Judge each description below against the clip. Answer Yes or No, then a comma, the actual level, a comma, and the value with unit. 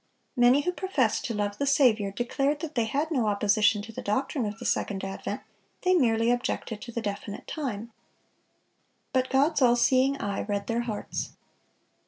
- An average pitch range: Yes, average, 4.6 semitones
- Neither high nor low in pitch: No, high, 235 Hz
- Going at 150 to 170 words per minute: No, average, 180 wpm